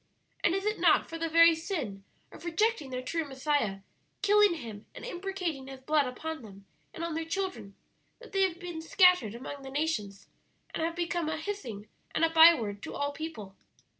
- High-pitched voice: Yes, very high, 320 Hz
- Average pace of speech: Yes, average, 190 wpm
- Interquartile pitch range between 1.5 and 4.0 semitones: No, wide, 5.4 semitones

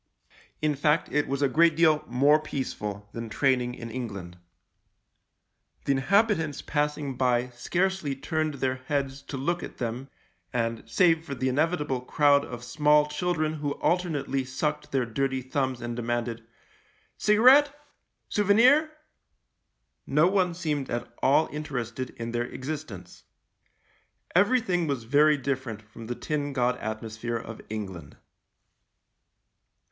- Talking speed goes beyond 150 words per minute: No, slow, 135 wpm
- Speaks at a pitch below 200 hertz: Yes, medium, 140 Hz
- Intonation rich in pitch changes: No, average, 4.3 semitones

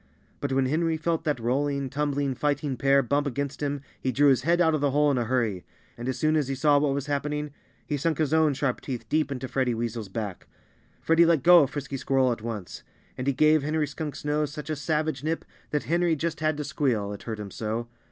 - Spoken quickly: Yes, fast, 235 wpm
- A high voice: No, medium, 140 Hz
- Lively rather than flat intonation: No, average, 2.9 semitones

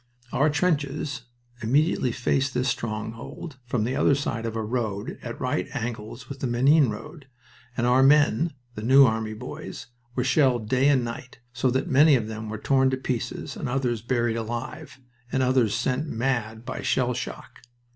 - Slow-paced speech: No, average, 175 wpm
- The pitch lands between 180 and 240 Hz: No, low, 125 Hz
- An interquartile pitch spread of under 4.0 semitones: Yes, average, 2.9 semitones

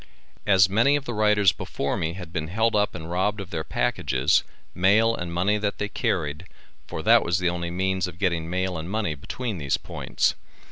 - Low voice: Yes, very low, 95 Hz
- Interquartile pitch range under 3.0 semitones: No, average, 3.4 semitones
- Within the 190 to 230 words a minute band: Yes, average, 200 wpm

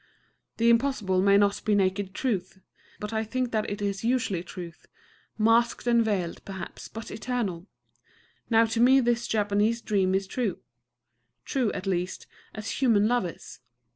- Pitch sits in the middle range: No, high, 215 Hz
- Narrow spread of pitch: No, average, 3.3 semitones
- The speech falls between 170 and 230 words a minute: No, average, 155 wpm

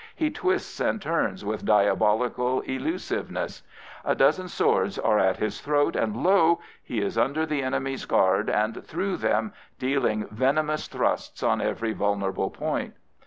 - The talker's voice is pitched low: Yes, low, 130 Hz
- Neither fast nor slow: Yes, average, 145 wpm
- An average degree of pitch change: No, wide, 6.9 semitones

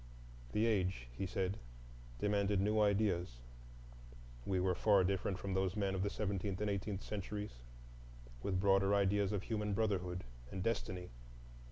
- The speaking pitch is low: Yes, very low, 95 Hz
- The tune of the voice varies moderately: No, narrow, 2.1 semitones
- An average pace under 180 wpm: Yes, average, 140 wpm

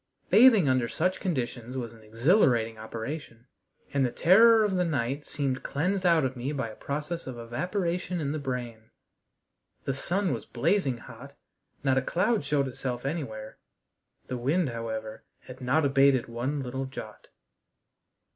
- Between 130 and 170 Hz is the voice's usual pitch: Yes, low, 135 Hz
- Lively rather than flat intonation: Yes, wide, 5.8 semitones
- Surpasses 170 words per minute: No, average, 155 wpm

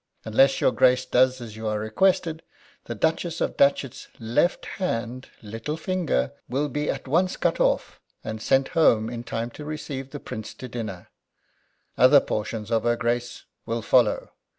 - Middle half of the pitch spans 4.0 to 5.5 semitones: Yes, average, 4.7 semitones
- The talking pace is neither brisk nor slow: Yes, average, 165 wpm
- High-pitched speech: No, low, 125 Hz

